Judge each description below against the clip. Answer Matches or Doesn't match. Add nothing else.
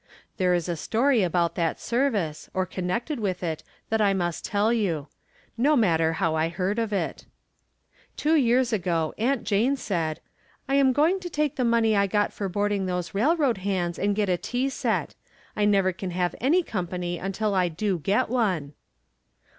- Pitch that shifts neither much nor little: Matches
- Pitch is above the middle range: Matches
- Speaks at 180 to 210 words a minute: Matches